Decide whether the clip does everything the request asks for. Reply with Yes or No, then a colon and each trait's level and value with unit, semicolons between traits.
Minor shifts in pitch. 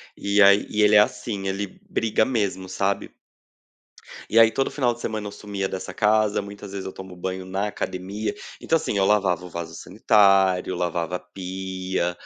Yes: narrow, 2.1 semitones